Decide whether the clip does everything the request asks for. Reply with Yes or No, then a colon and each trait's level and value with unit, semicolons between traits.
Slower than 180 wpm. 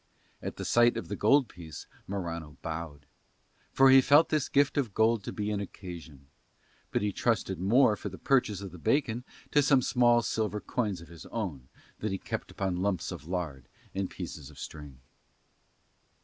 No: average, 185 wpm